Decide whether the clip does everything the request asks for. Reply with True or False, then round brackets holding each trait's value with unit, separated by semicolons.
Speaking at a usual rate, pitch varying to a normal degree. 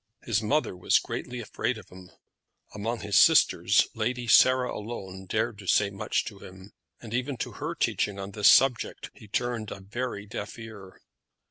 True (170 wpm; 3.4 semitones)